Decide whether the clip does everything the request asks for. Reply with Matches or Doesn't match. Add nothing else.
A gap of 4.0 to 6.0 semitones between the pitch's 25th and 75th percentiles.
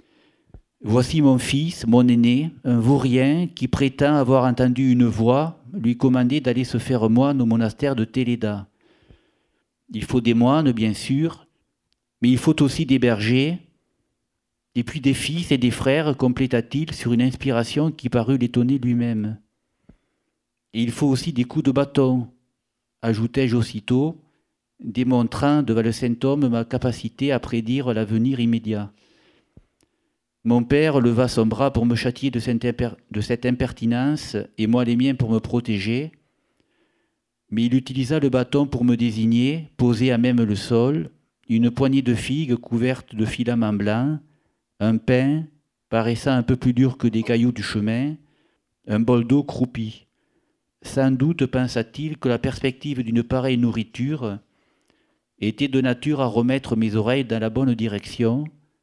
Doesn't match